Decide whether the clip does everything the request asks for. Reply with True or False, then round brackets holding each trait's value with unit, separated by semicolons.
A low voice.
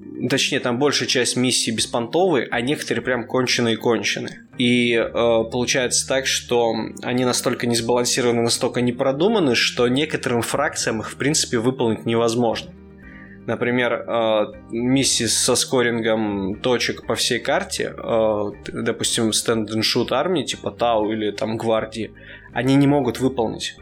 True (120 Hz)